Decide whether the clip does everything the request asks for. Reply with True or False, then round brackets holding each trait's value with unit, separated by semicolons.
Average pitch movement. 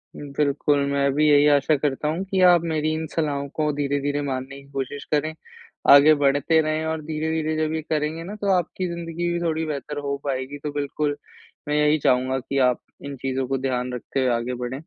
False (2.3 semitones)